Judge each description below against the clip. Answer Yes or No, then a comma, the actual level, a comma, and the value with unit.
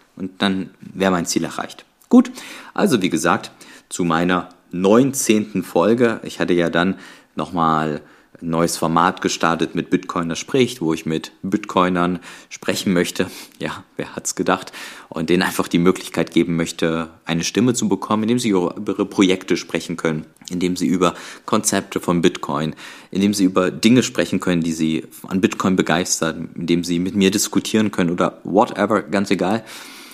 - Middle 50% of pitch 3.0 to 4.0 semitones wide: No, narrow, 2.5 semitones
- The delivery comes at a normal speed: Yes, average, 165 wpm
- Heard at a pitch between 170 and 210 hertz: No, very low, 90 Hz